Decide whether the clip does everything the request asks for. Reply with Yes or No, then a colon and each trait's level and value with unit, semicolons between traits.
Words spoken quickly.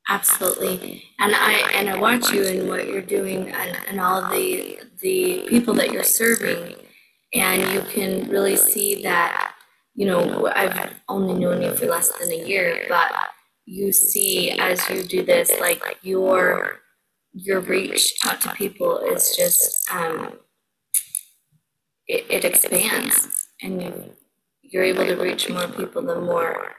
No: average, 145 wpm